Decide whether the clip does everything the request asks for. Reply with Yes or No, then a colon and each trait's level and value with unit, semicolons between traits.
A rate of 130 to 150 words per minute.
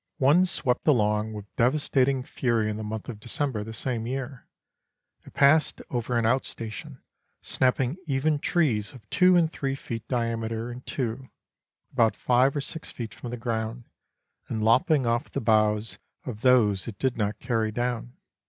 No: average, 170 wpm